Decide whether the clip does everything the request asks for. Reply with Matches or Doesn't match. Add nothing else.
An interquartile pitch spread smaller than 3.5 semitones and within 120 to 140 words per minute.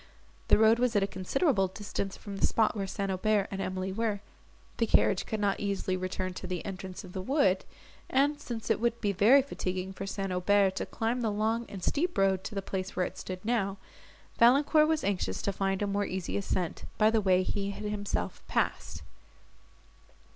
Doesn't match